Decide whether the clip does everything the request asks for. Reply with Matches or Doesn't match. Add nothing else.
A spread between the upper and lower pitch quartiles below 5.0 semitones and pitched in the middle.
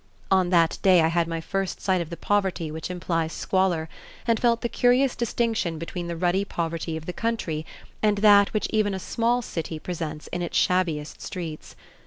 Matches